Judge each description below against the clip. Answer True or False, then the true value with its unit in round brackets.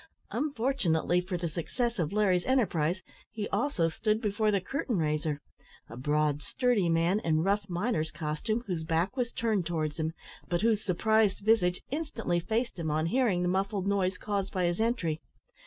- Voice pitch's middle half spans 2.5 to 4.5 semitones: False (5.0 semitones)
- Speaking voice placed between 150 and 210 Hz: True (185 Hz)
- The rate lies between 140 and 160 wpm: False (170 wpm)